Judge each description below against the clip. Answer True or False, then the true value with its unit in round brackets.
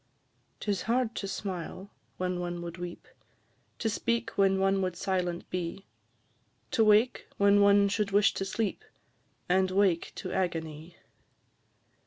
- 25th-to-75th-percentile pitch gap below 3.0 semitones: True (2.4 semitones)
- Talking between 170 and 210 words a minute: False (135 wpm)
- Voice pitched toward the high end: True (195 Hz)